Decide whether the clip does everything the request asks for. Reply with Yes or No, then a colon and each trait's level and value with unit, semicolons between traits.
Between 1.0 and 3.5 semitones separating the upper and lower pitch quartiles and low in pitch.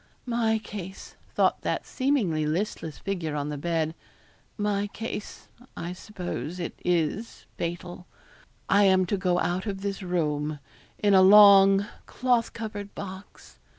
No: average, 3.1 semitones; high, 190 Hz